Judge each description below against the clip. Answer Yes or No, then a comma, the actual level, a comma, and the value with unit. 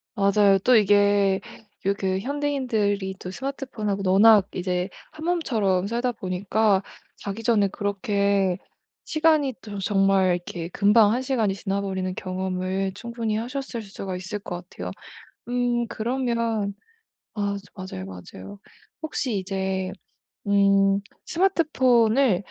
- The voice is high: Yes, high, 200 Hz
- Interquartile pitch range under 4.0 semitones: Yes, average, 3.6 semitones